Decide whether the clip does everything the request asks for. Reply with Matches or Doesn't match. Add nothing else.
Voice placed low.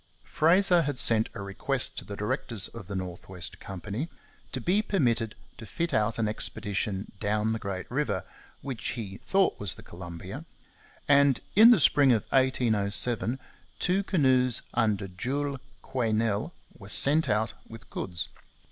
Matches